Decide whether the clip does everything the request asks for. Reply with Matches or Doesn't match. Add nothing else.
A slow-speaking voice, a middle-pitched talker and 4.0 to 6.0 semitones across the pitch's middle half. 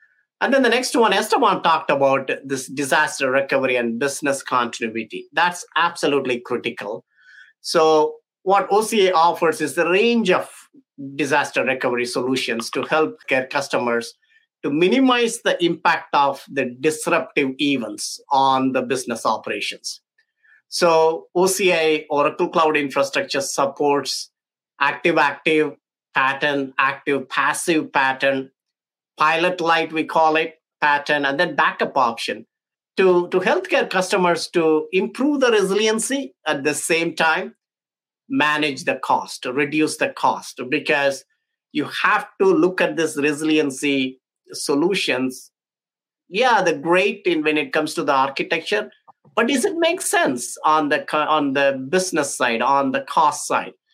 Matches